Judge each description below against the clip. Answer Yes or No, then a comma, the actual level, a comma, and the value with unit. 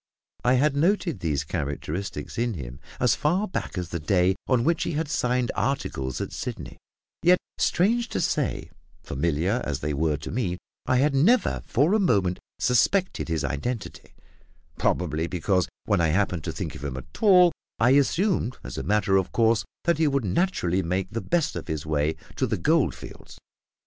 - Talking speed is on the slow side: No, average, 180 wpm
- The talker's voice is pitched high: No, low, 105 Hz